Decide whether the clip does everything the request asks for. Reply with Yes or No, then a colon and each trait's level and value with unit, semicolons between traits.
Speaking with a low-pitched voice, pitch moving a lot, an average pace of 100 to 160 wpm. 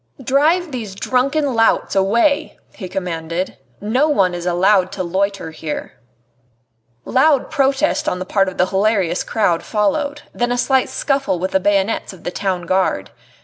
No: high, 205 Hz; wide, 6.4 semitones; average, 155 wpm